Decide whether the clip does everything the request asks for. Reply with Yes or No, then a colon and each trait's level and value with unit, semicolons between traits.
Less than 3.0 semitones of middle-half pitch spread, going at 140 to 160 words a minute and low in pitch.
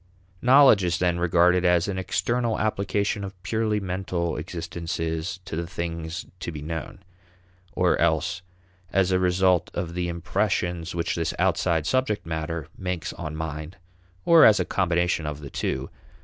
Yes: narrow, 2.4 semitones; average, 150 wpm; very low, 85 Hz